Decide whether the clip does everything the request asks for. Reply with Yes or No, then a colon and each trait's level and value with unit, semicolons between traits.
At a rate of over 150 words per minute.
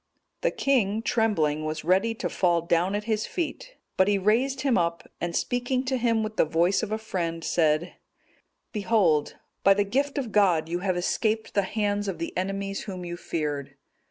Yes: average, 185 wpm